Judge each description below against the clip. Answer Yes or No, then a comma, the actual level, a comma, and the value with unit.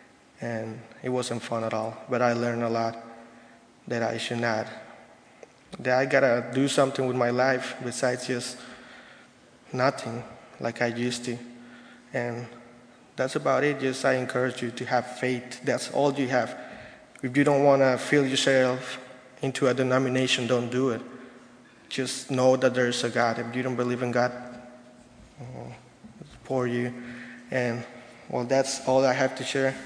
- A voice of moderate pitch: No, low, 125 Hz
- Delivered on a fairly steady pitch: Yes, narrow, 1.4 semitones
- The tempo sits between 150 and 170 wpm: Yes, average, 165 wpm